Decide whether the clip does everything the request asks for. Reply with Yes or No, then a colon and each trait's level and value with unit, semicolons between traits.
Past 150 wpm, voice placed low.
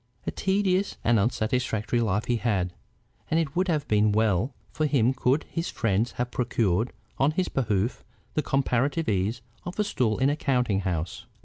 Yes: average, 175 wpm; low, 120 Hz